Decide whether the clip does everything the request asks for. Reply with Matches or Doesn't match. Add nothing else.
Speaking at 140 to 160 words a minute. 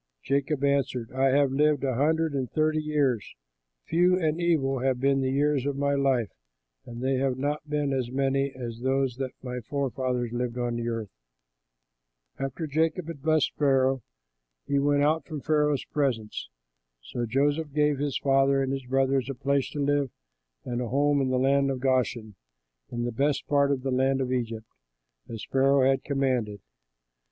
Doesn't match